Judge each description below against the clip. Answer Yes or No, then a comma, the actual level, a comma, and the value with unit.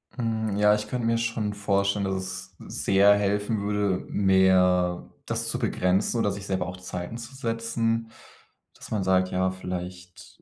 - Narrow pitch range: No, average, 3.0 semitones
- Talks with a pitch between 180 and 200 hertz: No, low, 100 Hz